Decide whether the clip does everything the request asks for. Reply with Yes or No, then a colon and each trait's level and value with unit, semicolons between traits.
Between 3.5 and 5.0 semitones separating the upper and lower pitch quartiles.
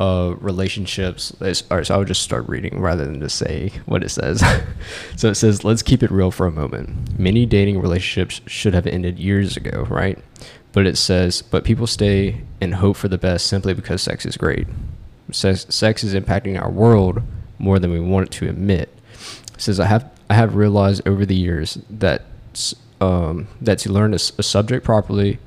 No: average, 2.8 semitones